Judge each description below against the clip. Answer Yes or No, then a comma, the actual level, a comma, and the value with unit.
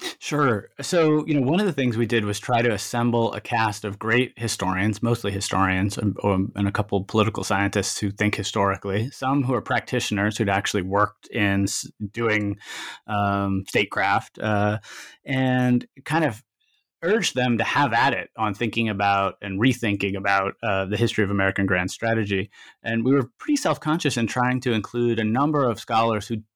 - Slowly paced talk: No, average, 180 wpm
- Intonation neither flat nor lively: Yes, average, 3.8 semitones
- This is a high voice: No, low, 110 Hz